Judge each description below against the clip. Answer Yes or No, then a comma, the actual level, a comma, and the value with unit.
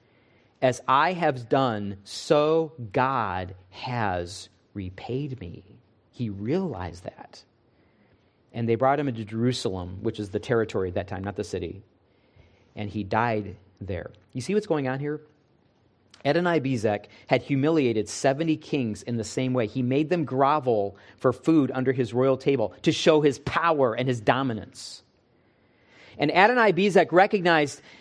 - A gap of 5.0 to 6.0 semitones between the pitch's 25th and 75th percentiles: Yes, average, 5.3 semitones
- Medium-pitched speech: No, low, 120 Hz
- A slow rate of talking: No, average, 150 wpm